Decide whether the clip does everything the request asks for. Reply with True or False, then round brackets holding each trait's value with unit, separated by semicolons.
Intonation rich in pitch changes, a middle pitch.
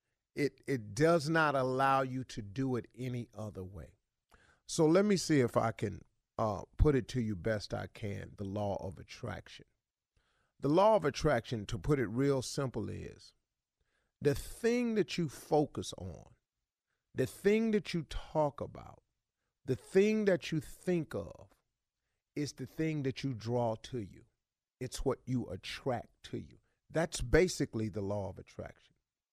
False (5.7 semitones; 130 Hz)